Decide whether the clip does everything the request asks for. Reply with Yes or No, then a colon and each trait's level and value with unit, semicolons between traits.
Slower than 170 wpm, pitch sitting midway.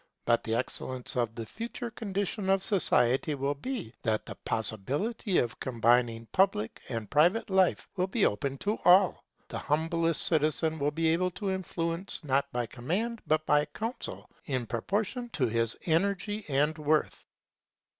Yes: average, 155 wpm; medium, 155 Hz